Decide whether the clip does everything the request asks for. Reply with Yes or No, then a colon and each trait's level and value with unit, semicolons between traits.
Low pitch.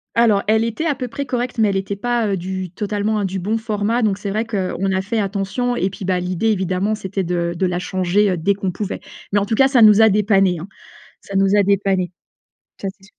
No: high, 200 Hz